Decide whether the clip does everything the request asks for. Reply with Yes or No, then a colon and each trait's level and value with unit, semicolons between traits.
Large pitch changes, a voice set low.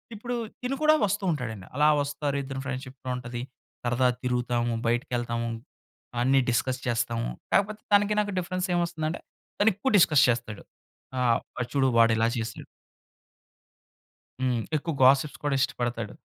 Yes: wide, 6.0 semitones; low, 130 Hz